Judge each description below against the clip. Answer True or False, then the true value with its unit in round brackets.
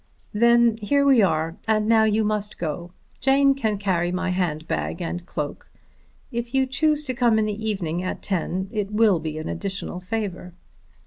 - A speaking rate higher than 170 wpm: True (180 wpm)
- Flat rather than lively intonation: False (4.5 semitones)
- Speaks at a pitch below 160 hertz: False (210 Hz)